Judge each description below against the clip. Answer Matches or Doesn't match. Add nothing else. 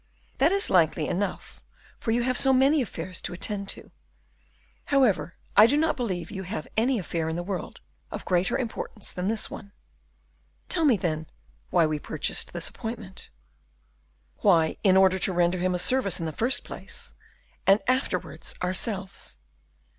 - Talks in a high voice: Matches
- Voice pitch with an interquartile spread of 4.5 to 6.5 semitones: Matches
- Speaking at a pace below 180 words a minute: Matches